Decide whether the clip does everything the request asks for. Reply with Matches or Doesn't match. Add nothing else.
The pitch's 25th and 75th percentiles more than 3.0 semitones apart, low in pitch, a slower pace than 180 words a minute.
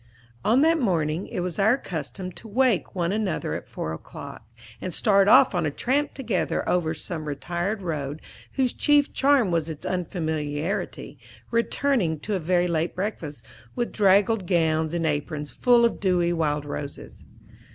Doesn't match